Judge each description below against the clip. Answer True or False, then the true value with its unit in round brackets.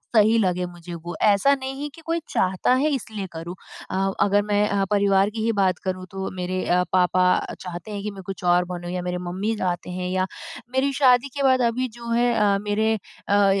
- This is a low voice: False (200 Hz)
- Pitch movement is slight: False (3.8 semitones)